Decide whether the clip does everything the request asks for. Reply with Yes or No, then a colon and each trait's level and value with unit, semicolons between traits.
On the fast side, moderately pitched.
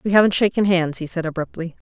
Yes: fast, 220 wpm; medium, 175 Hz